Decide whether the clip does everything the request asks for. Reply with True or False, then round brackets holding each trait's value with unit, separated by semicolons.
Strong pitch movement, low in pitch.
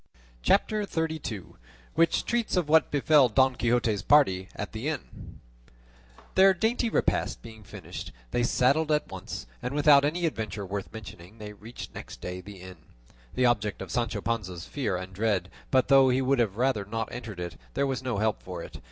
True (6.1 semitones; 115 Hz)